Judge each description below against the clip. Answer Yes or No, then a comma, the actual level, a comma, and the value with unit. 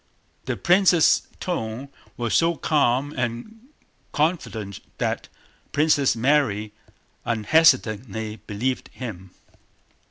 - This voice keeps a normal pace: No, slow, 85 wpm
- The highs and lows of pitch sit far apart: Yes, wide, 5.9 semitones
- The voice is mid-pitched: No, low, 125 Hz